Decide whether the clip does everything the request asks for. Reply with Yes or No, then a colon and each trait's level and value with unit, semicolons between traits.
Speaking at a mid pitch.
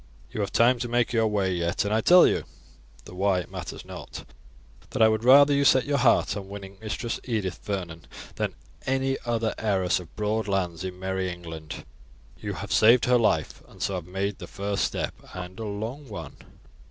No: low, 100 Hz